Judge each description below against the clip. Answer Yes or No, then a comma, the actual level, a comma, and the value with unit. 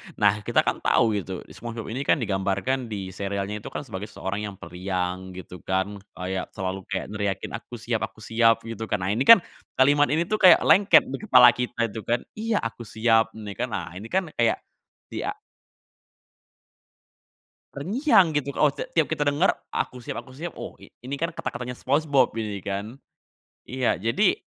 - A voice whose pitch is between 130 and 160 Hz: No, low, 115 Hz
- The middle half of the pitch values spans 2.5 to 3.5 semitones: No, wide, 5.6 semitones